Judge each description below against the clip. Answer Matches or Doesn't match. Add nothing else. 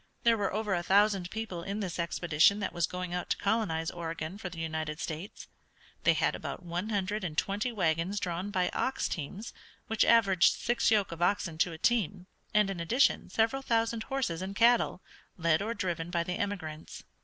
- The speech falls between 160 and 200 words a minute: Matches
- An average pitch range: Matches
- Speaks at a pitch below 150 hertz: Doesn't match